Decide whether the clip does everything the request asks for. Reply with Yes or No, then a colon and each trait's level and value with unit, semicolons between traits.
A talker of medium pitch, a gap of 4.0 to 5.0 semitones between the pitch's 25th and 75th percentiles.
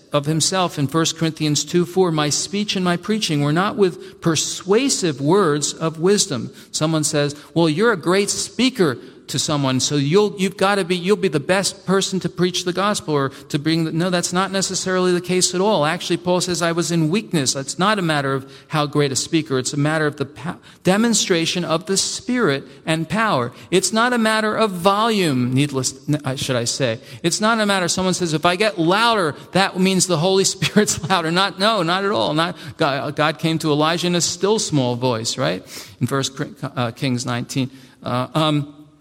Yes: medium, 170 Hz; average, 4.7 semitones